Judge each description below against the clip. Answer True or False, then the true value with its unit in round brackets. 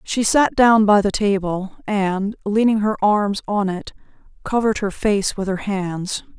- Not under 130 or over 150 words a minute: False (170 wpm)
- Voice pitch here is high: True (205 Hz)